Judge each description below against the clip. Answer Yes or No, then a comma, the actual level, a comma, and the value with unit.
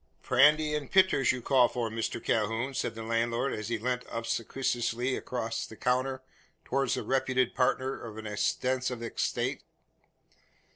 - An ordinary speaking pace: Yes, average, 145 wpm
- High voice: No, low, 125 Hz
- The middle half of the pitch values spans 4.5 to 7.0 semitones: No, narrow, 2.5 semitones